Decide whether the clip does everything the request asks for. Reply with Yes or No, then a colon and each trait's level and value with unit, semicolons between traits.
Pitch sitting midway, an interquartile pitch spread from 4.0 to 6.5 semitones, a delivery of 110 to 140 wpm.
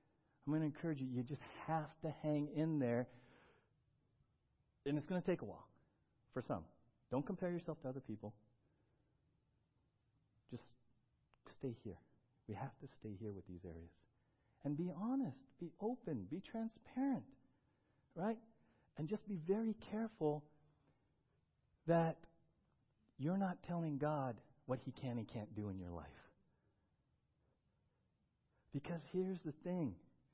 Yes: medium, 145 Hz; wide, 5.5 semitones; slow, 135 wpm